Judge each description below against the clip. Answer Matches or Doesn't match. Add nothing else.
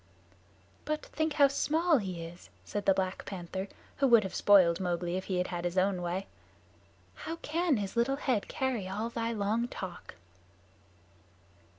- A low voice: Doesn't match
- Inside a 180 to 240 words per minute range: Doesn't match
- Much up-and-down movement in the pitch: Matches